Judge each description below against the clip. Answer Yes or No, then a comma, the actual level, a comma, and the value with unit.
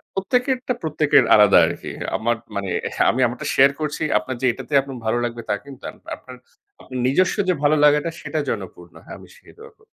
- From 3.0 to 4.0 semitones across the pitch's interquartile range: No, average, 5.2 semitones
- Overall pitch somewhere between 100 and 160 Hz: Yes, low, 135 Hz